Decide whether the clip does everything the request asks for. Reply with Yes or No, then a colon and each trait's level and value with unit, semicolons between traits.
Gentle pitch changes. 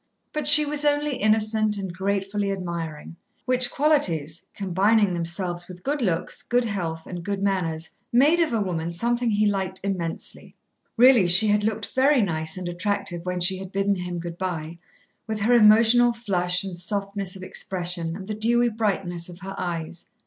No: average, 4.0 semitones